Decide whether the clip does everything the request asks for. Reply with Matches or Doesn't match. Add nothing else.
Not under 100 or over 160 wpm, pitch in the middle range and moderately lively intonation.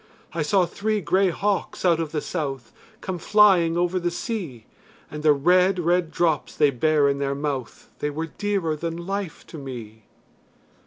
Doesn't match